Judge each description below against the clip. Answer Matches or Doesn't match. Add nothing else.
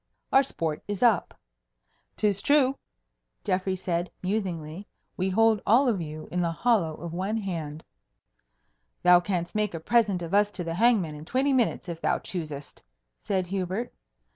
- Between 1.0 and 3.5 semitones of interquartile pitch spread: Doesn't match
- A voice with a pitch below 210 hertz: Matches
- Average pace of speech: Matches